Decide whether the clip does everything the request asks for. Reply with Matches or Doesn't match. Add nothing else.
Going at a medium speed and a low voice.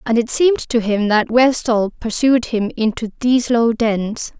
Doesn't match